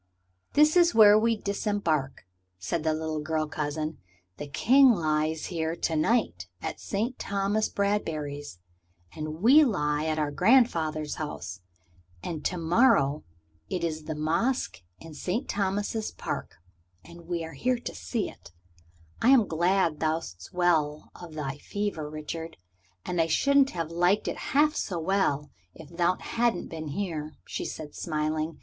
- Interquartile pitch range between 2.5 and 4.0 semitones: No, average, 5.0 semitones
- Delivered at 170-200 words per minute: No, average, 145 wpm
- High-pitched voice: No, medium, 165 Hz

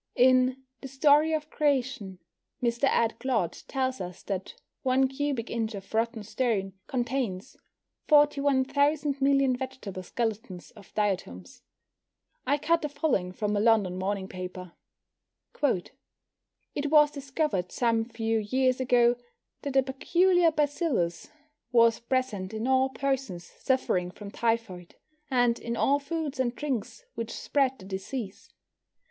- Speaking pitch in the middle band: No, very high, 250 Hz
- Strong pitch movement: No, average, 4.9 semitones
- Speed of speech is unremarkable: No, slow, 130 wpm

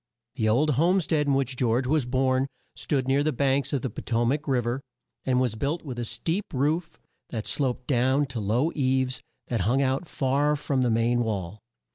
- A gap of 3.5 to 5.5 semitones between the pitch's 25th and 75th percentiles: No, average, 3.0 semitones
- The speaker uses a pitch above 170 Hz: No, low, 130 Hz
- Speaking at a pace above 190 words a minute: Yes, fast, 205 wpm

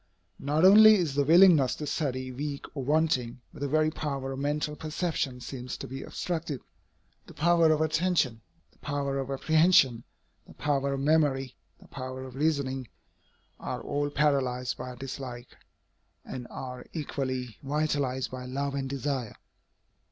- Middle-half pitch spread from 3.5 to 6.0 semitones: No, average, 2.9 semitones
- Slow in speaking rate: No, average, 150 wpm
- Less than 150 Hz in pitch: Yes, medium, 140 Hz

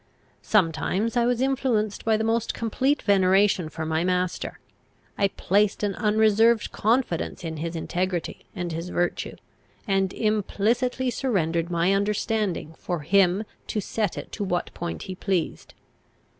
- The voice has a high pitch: Yes, high, 195 Hz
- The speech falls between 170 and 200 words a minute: No, average, 140 wpm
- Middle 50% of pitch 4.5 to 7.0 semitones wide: No, average, 3.9 semitones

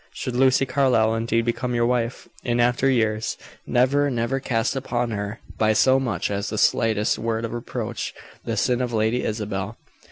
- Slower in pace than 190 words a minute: Yes, average, 170 wpm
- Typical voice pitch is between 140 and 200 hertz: No, low, 120 Hz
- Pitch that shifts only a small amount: Yes, narrow, 2.2 semitones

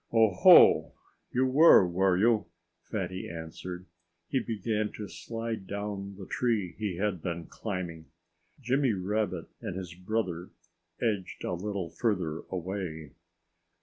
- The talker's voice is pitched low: Yes, very low, 95 Hz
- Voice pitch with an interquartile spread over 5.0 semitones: No, average, 3.6 semitones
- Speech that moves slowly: Yes, slow, 125 wpm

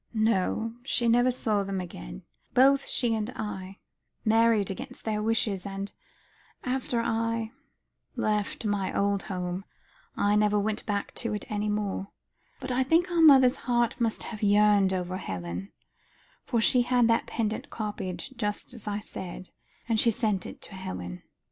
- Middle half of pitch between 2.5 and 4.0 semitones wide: Yes, average, 2.9 semitones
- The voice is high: Yes, high, 210 Hz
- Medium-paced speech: Yes, average, 155 wpm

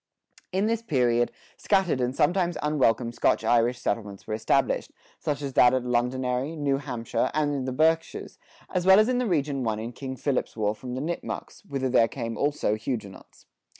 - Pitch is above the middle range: No, low, 130 Hz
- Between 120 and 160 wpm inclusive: No, average, 185 wpm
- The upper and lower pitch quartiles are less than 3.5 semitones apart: No, average, 4.3 semitones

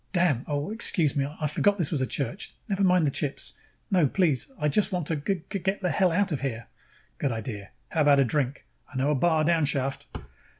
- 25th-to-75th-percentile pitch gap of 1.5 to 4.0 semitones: No, average, 4.7 semitones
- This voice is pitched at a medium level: Yes, medium, 150 Hz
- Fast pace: Yes, fast, 220 wpm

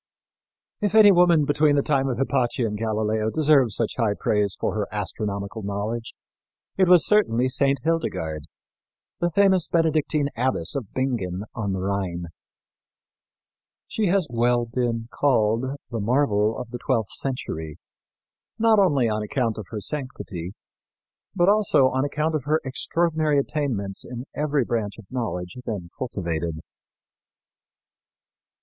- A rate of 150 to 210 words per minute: No, slow, 135 wpm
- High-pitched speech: No, low, 125 Hz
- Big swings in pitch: Yes, wide, 6.0 semitones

